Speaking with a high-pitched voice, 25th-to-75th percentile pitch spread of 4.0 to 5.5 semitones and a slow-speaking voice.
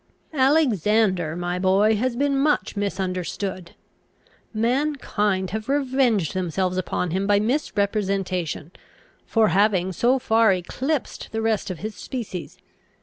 Yes: high, 205 Hz; average, 4.3 semitones; slow, 115 wpm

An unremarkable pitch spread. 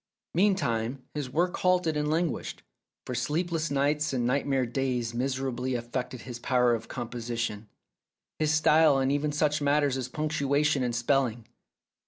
Yes: average, 3.7 semitones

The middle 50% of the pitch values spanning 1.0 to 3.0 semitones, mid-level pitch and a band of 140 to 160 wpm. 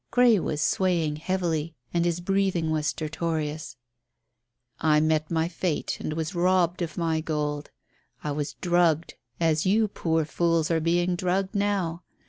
Yes: narrow, 2.4 semitones; medium, 165 Hz; average, 145 wpm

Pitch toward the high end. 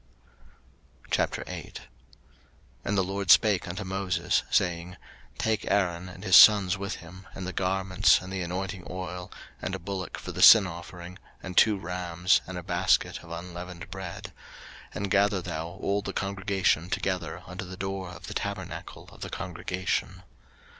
No: very low, 95 Hz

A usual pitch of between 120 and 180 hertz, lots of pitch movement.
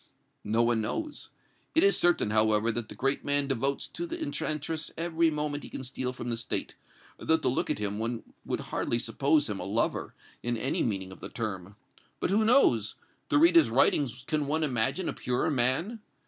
Yes: low, 135 Hz; wide, 5.9 semitones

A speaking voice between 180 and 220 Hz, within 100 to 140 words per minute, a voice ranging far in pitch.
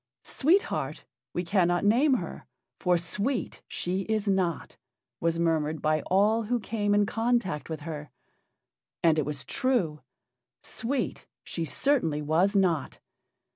Yes: medium, 185 Hz; slow, 135 wpm; wide, 5.7 semitones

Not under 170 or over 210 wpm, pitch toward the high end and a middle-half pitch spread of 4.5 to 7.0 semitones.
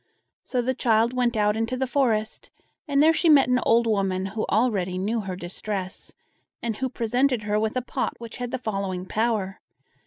No: average, 190 wpm; high, 225 Hz; average, 3.7 semitones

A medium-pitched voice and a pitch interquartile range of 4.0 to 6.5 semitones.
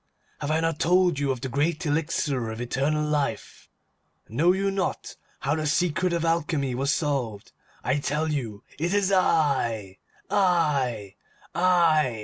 Yes: medium, 150 Hz; average, 4.5 semitones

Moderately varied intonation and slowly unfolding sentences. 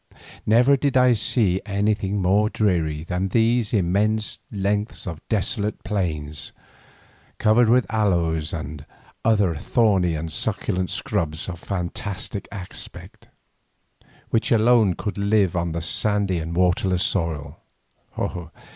Yes: average, 4.0 semitones; slow, 115 wpm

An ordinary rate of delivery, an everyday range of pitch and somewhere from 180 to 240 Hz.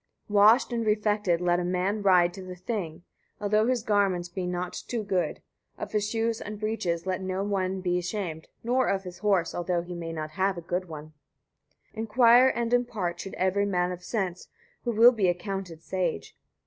Yes: average, 190 wpm; average, 3.2 semitones; high, 190 Hz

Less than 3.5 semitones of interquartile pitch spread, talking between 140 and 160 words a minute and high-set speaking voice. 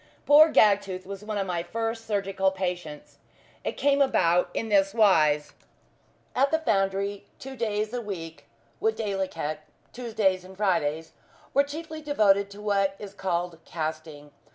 No: average, 3.8 semitones; average, 145 wpm; high, 200 Hz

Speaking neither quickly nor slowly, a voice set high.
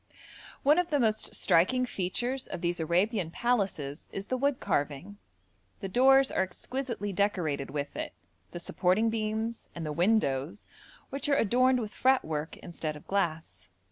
Yes: average, 150 wpm; high, 200 Hz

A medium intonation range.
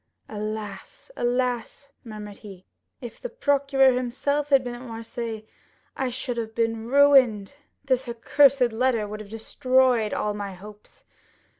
Yes: average, 3.5 semitones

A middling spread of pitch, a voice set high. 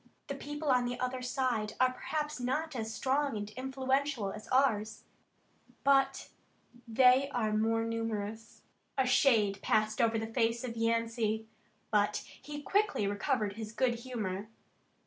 Yes: average, 3.4 semitones; high, 235 Hz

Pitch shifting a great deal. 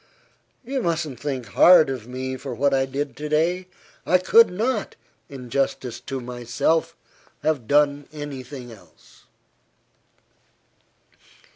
No: average, 3.7 semitones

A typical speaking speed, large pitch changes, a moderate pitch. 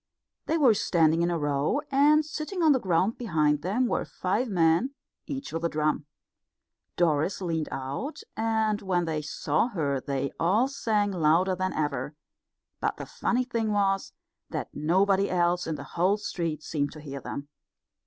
Yes: average, 165 wpm; wide, 6.2 semitones; medium, 180 Hz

